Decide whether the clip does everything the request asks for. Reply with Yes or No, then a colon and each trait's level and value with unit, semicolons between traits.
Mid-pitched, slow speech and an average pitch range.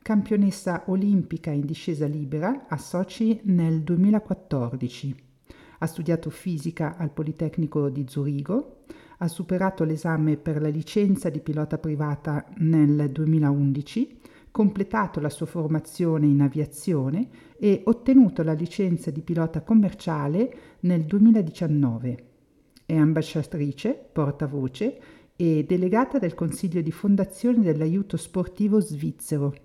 Yes: medium, 165 Hz; slow, 110 wpm; average, 4.3 semitones